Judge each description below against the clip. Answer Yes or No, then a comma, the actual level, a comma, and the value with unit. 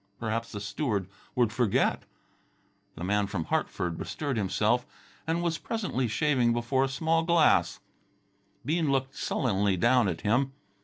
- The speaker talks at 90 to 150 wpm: Yes, average, 140 wpm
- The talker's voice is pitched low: Yes, low, 125 Hz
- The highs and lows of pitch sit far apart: Yes, wide, 5.7 semitones